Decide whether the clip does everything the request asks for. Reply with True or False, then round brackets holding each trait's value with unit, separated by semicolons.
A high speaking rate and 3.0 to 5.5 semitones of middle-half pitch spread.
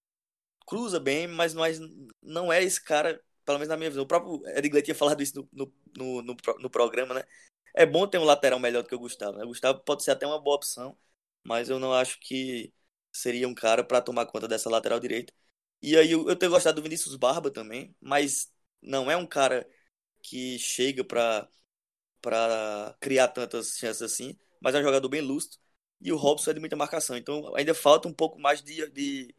True (205 wpm; 4.1 semitones)